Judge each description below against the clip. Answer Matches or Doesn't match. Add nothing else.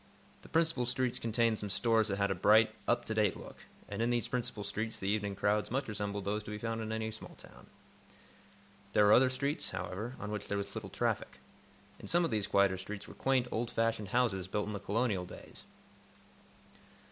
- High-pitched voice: Doesn't match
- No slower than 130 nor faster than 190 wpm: Doesn't match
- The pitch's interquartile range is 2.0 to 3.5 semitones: Matches